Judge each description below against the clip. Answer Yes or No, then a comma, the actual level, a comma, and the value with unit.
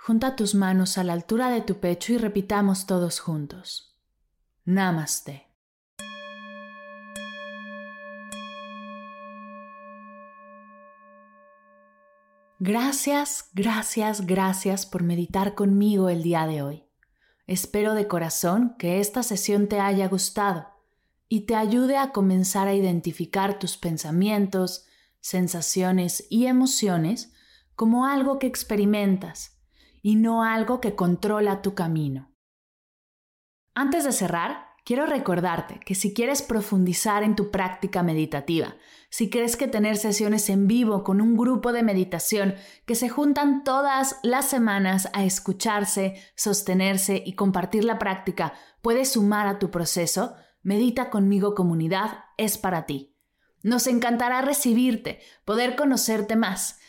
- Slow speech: Yes, slow, 115 wpm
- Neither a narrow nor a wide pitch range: Yes, average, 4.6 semitones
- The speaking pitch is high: Yes, high, 195 Hz